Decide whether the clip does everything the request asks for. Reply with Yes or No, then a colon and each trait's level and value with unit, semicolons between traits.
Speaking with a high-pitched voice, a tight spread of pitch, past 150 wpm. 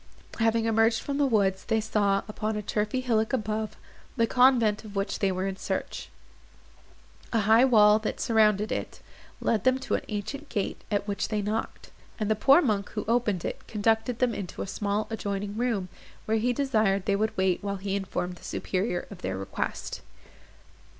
Yes: high, 215 Hz; narrow, 2.2 semitones; average, 185 wpm